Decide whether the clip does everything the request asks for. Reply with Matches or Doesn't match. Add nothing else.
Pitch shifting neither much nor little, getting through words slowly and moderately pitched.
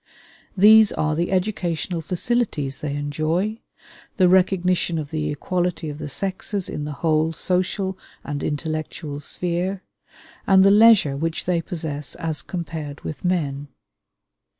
Matches